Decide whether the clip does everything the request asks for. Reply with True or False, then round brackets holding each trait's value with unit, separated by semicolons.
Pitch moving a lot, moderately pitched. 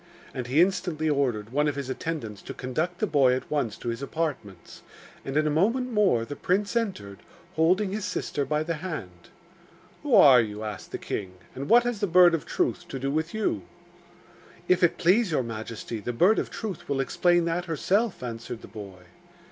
True (6.9 semitones; 155 Hz)